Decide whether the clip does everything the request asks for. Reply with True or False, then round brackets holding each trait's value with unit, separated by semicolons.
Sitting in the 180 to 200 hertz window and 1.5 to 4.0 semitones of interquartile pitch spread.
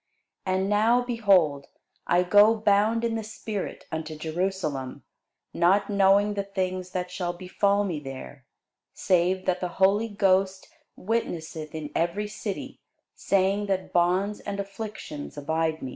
True (190 Hz; 3.0 semitones)